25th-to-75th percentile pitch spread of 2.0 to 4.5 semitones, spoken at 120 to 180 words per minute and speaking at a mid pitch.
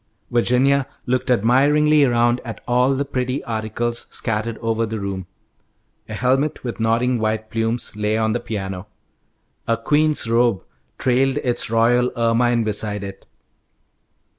No: narrow, 2.4 semitones; slow, 135 wpm; low, 120 Hz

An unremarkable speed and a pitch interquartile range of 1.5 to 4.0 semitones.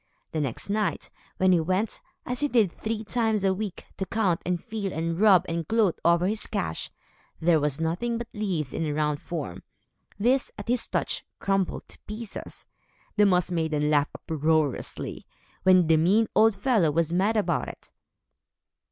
No: average, 170 wpm; average, 5.0 semitones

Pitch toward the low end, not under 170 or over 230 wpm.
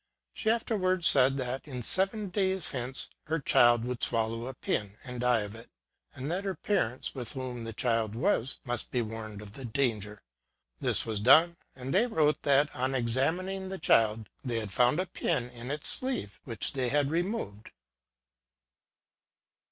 Yes: low, 130 Hz; average, 175 wpm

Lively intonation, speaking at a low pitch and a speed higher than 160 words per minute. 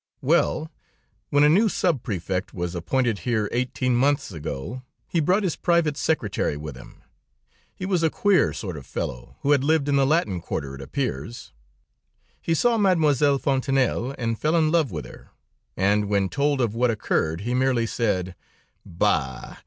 Yes: wide, 7.8 semitones; low, 130 Hz; average, 170 wpm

